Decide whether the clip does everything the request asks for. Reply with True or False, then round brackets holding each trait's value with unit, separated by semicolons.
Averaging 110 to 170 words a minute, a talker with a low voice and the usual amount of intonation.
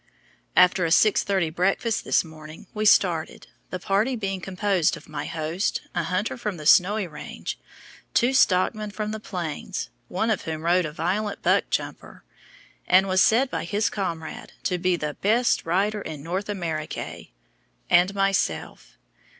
False (155 wpm; 185 Hz; 3.8 semitones)